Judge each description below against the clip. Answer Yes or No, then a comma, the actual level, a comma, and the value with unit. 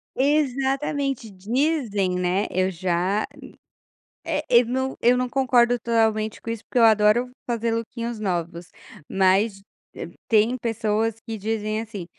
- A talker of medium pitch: No, high, 225 Hz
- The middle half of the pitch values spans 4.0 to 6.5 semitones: No, average, 3.3 semitones